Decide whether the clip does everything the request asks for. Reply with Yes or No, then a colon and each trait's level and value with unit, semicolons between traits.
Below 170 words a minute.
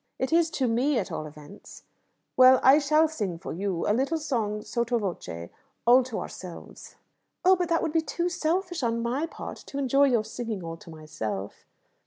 No: average, 190 wpm